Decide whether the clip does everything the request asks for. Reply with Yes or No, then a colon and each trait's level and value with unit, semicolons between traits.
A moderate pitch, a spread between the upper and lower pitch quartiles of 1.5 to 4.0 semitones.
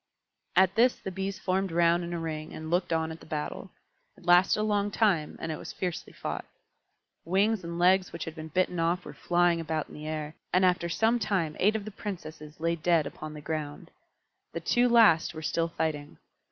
Yes: medium, 170 Hz; average, 3.2 semitones